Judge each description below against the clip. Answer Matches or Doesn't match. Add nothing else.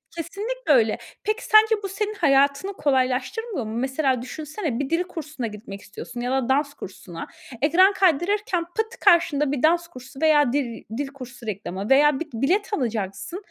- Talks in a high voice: Matches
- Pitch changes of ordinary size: Doesn't match